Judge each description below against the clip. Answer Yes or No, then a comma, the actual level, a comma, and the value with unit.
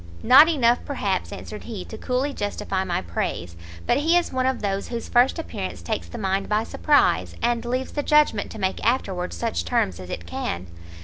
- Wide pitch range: Yes, wide, 6.3 semitones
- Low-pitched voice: No, high, 215 Hz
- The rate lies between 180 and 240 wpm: Yes, average, 195 wpm